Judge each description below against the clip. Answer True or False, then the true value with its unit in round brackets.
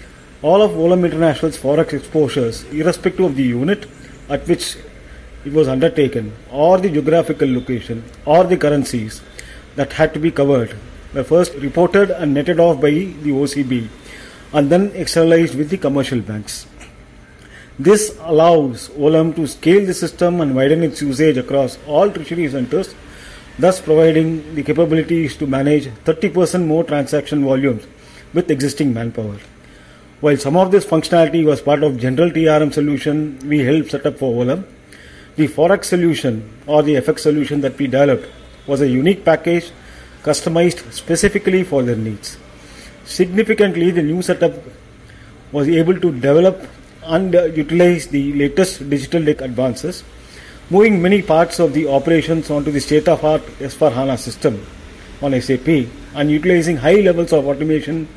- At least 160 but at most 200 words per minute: False (150 wpm)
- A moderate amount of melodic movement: True (3.8 semitones)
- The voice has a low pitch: False (150 Hz)